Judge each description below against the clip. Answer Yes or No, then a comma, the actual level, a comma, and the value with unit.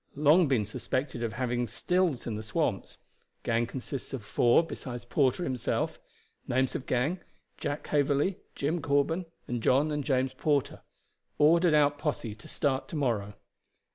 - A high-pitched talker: No, low, 135 Hz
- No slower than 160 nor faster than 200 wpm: No, average, 150 wpm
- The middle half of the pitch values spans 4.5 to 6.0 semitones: No, average, 3.6 semitones